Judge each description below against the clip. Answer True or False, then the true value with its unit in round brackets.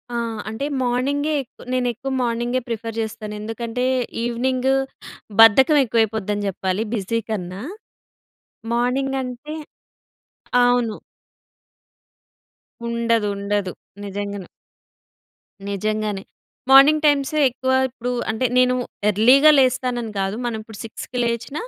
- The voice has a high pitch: True (235 Hz)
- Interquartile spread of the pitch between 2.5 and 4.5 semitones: True (3.1 semitones)